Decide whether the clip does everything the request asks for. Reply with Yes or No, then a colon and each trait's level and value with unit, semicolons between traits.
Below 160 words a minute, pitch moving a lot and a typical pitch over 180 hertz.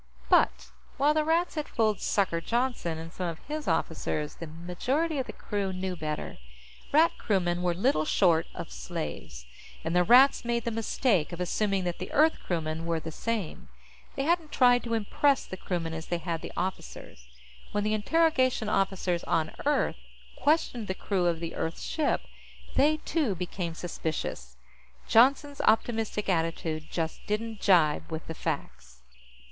No: average, 165 wpm; wide, 6.9 semitones; high, 190 Hz